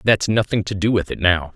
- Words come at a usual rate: No, fast, 270 wpm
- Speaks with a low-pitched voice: Yes, very low, 95 Hz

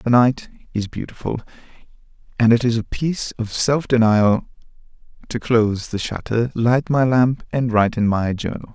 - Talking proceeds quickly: No, average, 165 wpm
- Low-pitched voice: Yes, low, 115 Hz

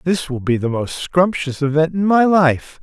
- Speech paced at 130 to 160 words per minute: No, fast, 215 wpm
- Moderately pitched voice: Yes, medium, 160 Hz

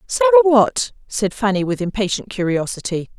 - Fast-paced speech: No, slow, 130 wpm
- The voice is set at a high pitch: Yes, high, 230 Hz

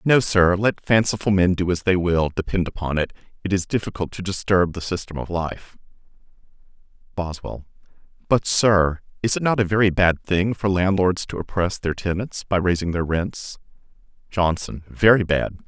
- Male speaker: Yes, male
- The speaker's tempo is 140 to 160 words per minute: No, average, 170 wpm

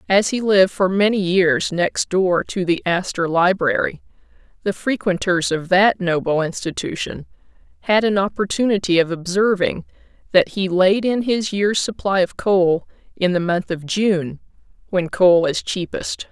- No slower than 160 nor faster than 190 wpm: No, average, 150 wpm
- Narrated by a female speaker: Yes, female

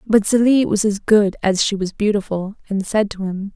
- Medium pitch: No, high, 205 Hz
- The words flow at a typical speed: No, fast, 220 wpm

